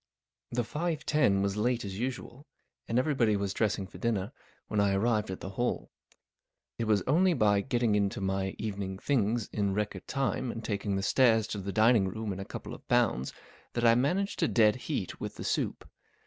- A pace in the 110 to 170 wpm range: No, fast, 205 wpm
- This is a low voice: Yes, low, 110 Hz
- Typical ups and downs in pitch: Yes, average, 3.7 semitones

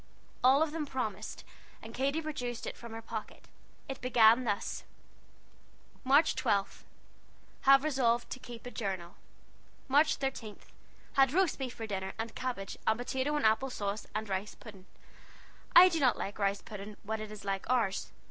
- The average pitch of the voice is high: Yes, high, 235 Hz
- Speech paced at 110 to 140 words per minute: No, average, 165 wpm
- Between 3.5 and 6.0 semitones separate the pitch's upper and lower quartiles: Yes, average, 4.3 semitones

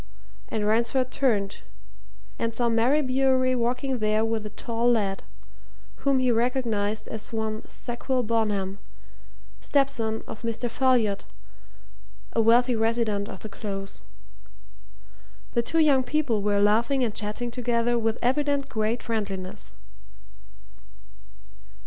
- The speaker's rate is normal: No, slow, 120 wpm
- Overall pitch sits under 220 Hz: No, high, 230 Hz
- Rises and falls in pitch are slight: No, average, 3.0 semitones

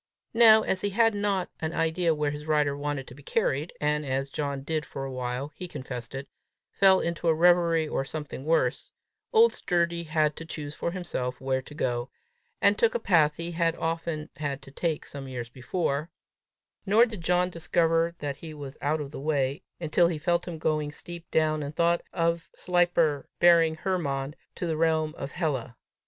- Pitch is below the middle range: No, medium, 155 Hz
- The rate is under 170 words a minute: No, average, 190 wpm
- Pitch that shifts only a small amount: No, average, 3.3 semitones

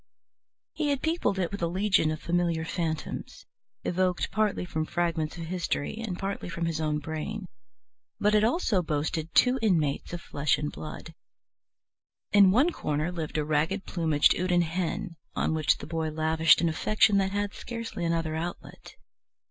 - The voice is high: No, medium, 170 Hz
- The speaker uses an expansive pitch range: No, average, 4.0 semitones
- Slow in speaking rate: No, average, 165 wpm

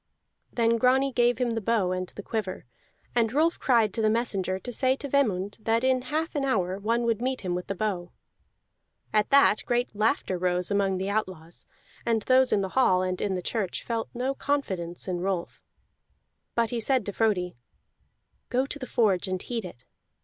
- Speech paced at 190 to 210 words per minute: Yes, average, 195 wpm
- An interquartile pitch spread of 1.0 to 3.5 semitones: No, average, 4.9 semitones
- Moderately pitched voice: No, high, 220 Hz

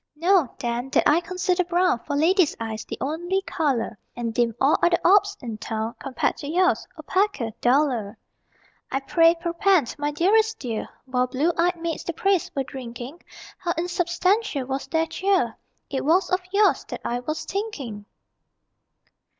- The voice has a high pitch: Yes, very high, 315 Hz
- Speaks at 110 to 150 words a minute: No, average, 160 wpm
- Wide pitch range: Yes, wide, 6.4 semitones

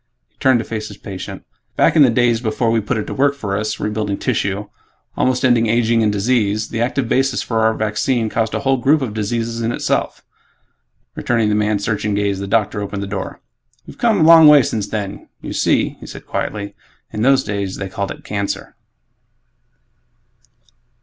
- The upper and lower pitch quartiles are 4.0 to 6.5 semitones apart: No, average, 2.9 semitones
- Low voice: Yes, low, 110 Hz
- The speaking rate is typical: Yes, average, 195 wpm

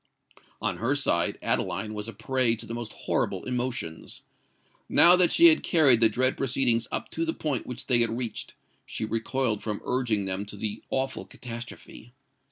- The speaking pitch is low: Yes, low, 120 Hz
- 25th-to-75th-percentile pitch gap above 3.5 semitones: No, average, 3.2 semitones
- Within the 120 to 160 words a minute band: No, average, 175 wpm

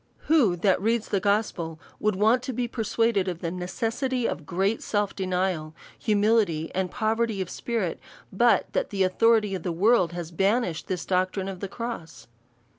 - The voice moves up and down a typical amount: Yes, average, 3.9 semitones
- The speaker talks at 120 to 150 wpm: No, average, 175 wpm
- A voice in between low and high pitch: No, high, 200 Hz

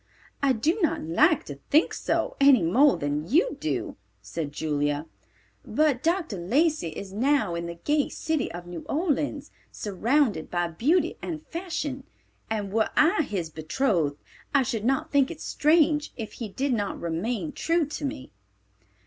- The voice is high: Yes, very high, 260 Hz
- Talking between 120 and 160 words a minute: Yes, average, 155 wpm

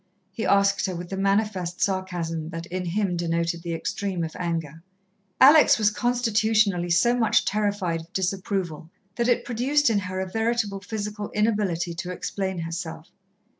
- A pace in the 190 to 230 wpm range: No, average, 155 wpm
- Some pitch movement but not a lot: Yes, average, 3.7 semitones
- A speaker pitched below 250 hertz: Yes, high, 190 Hz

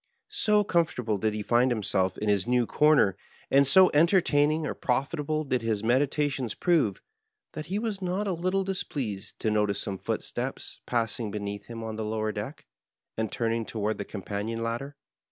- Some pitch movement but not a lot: No, wide, 6.3 semitones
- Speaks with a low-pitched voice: Yes, low, 120 Hz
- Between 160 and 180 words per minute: Yes, average, 170 wpm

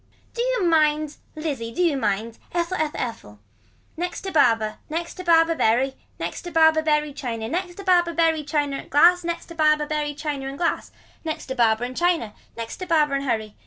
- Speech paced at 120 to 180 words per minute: No, average, 195 wpm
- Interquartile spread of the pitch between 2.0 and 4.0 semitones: No, average, 4.4 semitones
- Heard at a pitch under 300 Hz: No, very high, 305 Hz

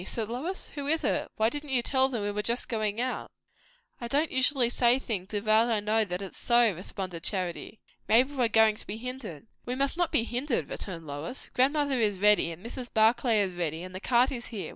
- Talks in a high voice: Yes, high, 230 Hz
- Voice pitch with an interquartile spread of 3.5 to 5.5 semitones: Yes, average, 4.0 semitones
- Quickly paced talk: Yes, fast, 220 wpm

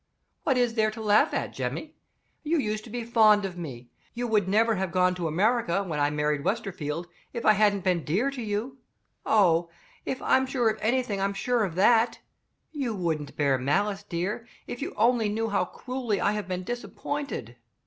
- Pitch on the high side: Yes, high, 210 Hz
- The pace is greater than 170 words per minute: Yes, average, 190 wpm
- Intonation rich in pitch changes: No, average, 4.8 semitones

